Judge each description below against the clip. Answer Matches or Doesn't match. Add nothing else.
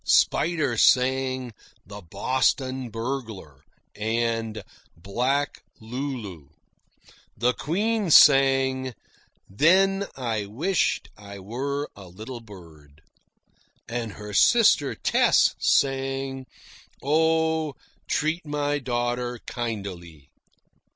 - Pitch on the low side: Matches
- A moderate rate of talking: Doesn't match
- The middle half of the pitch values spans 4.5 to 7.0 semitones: Matches